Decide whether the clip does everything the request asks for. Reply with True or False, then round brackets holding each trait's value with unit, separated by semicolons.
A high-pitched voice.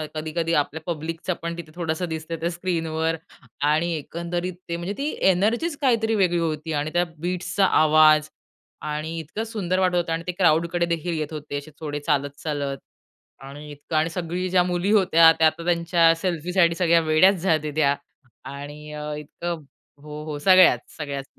False (165 Hz)